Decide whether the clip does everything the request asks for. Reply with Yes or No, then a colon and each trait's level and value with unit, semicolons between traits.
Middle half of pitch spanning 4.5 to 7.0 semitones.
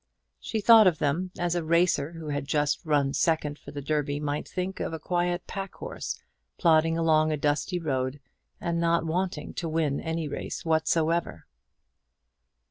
No: average, 2.7 semitones